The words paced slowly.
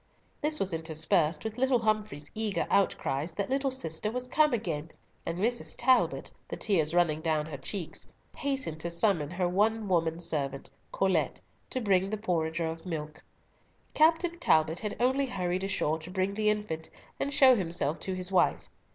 No: average, 170 wpm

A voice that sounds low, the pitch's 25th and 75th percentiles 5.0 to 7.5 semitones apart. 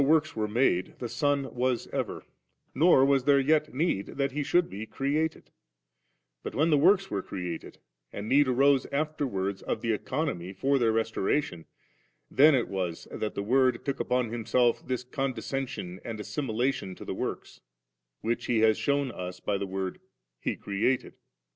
Yes: low, 125 Hz; average, 5.3 semitones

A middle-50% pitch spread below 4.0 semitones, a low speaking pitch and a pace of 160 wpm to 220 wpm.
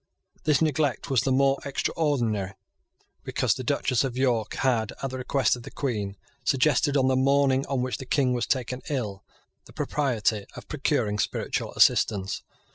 Yes: average, 3.4 semitones; low, 130 Hz; average, 165 wpm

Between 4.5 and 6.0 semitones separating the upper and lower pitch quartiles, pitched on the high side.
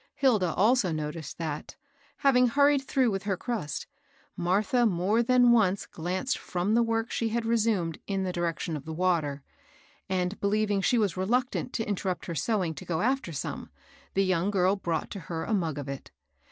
Yes: average, 5.1 semitones; high, 195 Hz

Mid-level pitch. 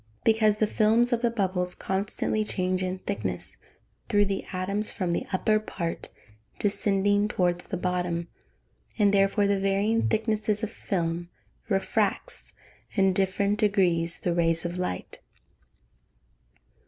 No: high, 195 Hz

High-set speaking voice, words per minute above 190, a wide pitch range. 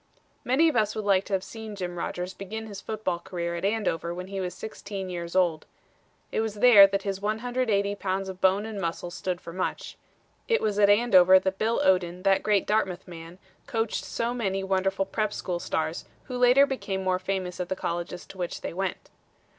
No: high, 195 Hz; average, 200 wpm; average, 2.8 semitones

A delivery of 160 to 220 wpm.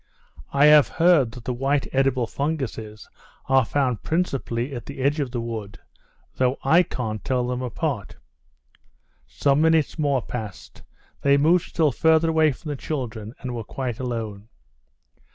No: average, 150 wpm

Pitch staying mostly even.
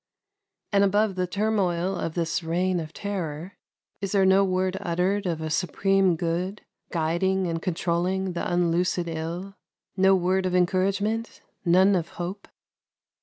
Yes: narrow, 2.2 semitones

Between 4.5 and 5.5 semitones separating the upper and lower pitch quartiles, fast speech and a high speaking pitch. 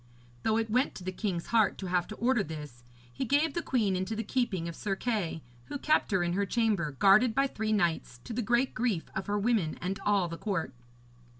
Yes: average, 4.8 semitones; fast, 225 wpm; high, 205 Hz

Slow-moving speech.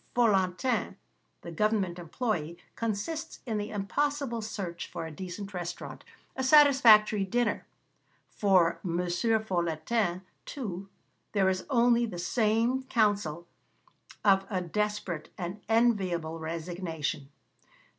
Yes: slow, 105 wpm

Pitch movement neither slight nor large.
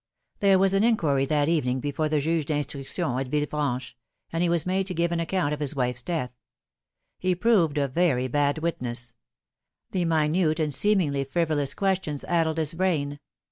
Yes: average, 3.6 semitones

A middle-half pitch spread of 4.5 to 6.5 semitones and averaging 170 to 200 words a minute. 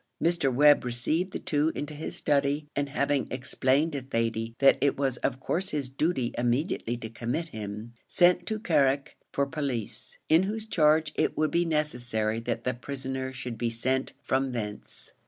No: average, 4.0 semitones; average, 175 wpm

